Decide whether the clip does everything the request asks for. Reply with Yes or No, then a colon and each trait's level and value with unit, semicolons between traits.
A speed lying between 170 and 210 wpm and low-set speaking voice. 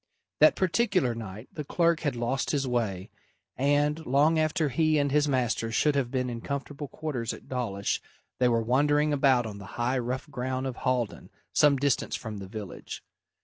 Yes: average, 180 wpm; low, 130 Hz